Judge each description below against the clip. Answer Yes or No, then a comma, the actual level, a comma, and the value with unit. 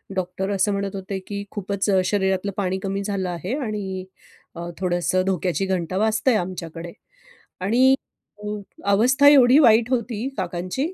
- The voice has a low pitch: No, high, 195 Hz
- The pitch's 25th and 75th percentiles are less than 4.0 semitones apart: Yes, average, 2.8 semitones